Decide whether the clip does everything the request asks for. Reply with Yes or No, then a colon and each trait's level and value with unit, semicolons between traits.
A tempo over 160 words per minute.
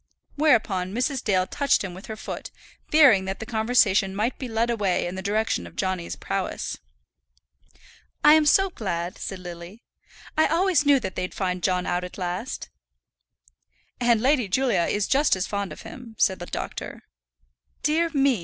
Yes: average, 170 wpm